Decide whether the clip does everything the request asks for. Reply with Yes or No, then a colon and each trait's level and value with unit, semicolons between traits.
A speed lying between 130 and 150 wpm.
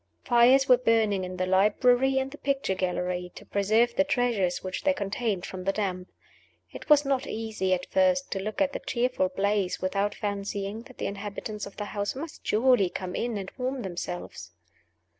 No: average, 185 wpm